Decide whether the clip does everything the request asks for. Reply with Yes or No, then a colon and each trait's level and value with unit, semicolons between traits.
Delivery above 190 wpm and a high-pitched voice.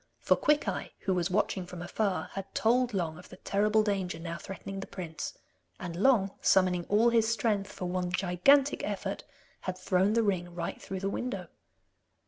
No: average, 175 wpm; high, 195 Hz